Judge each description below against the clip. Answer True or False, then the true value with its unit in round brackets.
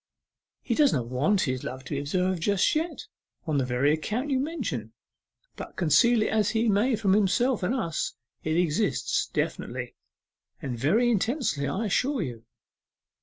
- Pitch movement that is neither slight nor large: False (8.9 semitones)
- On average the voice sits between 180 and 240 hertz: True (190 Hz)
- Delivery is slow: False (165 wpm)